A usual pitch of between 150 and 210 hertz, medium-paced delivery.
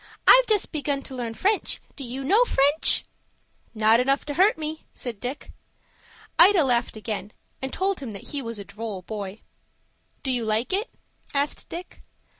No: very high, 265 Hz; average, 170 wpm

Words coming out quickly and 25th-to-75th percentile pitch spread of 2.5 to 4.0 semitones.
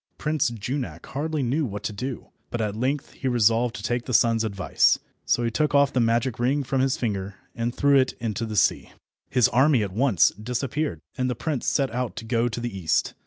Yes: fast, 215 wpm; average, 3.2 semitones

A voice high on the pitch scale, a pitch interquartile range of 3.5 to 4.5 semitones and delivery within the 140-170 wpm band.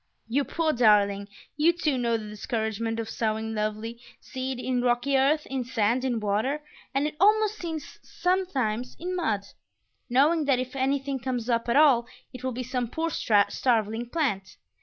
Yes: very high, 250 Hz; average, 4.1 semitones; average, 165 wpm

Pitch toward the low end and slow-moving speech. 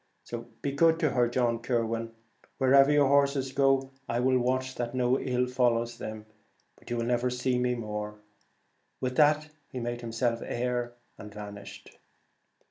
No: low, 125 Hz; average, 160 wpm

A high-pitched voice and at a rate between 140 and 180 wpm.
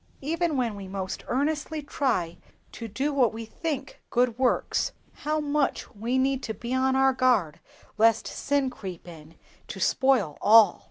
Yes: very high, 255 Hz; average, 160 wpm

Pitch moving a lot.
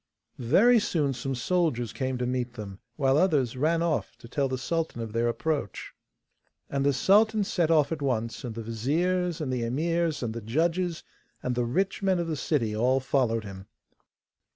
Yes: wide, 5.9 semitones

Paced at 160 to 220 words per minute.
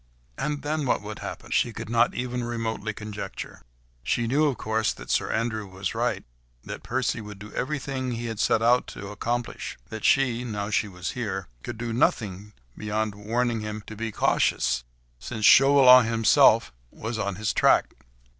Yes: average, 165 wpm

